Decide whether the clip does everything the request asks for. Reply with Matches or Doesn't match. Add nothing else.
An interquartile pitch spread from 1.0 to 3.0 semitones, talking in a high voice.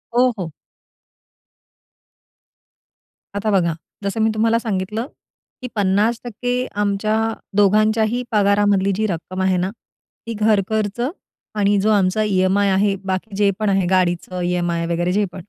Matches